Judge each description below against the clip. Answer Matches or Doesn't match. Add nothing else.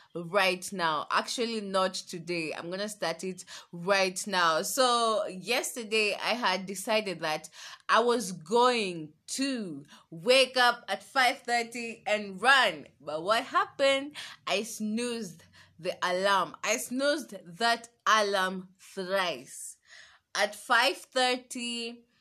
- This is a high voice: Matches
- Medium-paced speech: Doesn't match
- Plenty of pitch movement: Doesn't match